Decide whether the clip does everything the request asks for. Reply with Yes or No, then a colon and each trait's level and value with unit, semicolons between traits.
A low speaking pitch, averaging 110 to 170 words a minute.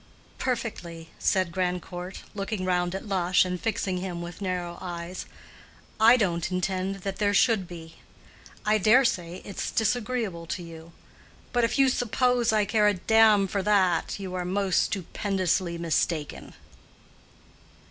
No: high, 190 Hz; average, 140 wpm